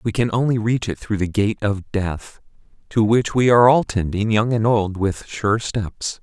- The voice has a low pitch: Yes, low, 110 Hz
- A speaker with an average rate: No, fast, 210 wpm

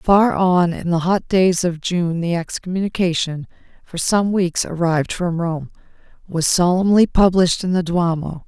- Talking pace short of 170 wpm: Yes, average, 155 wpm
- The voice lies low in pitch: No, medium, 175 Hz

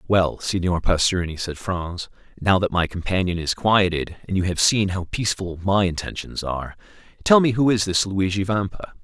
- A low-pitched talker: Yes, very low, 95 Hz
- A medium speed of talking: Yes, average, 180 wpm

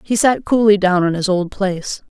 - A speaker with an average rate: No, fast, 230 wpm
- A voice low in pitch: No, high, 195 Hz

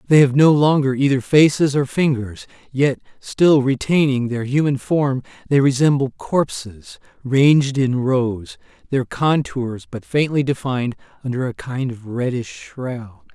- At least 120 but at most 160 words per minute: Yes, average, 140 wpm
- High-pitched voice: No, low, 135 Hz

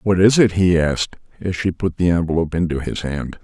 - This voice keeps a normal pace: No, fast, 225 wpm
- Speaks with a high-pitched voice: No, very low, 85 Hz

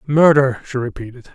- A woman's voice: No, male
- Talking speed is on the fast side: No, slow, 135 wpm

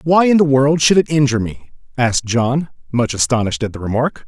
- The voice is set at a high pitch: No, low, 130 Hz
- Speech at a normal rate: No, fast, 210 wpm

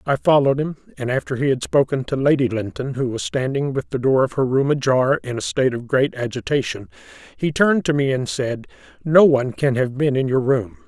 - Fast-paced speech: Yes, fast, 225 wpm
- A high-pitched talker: No, low, 135 Hz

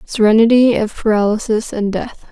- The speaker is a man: No, female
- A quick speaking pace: No, slow, 130 wpm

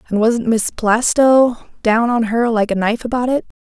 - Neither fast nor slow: Yes, average, 195 wpm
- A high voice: Yes, high, 230 Hz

